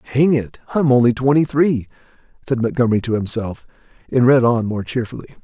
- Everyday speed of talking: Yes, average, 165 wpm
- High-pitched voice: No, low, 125 Hz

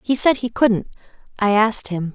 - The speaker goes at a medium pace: Yes, average, 170 wpm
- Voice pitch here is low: No, high, 220 Hz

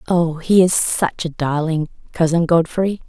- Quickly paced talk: No, average, 155 wpm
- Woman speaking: Yes, female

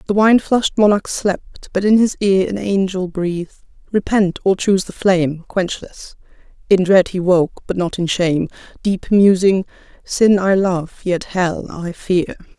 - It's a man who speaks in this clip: No, female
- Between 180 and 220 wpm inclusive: No, average, 155 wpm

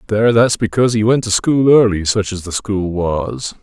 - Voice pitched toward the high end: No, low, 105 Hz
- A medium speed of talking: No, fast, 215 wpm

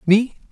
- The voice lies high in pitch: Yes, high, 210 Hz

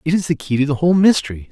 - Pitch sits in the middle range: Yes, medium, 150 Hz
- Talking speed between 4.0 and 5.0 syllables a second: No, 7.8 syllables/s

